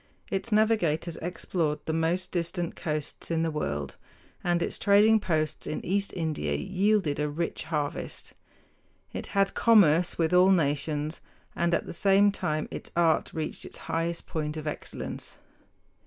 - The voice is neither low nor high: Yes, medium, 170 Hz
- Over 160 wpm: No, average, 150 wpm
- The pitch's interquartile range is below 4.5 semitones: Yes, average, 3.8 semitones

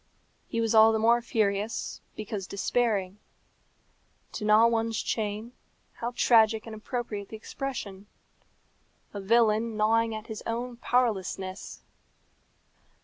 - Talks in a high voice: Yes, high, 220 Hz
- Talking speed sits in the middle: No, slow, 115 wpm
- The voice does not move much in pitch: Yes, narrow, 1.8 semitones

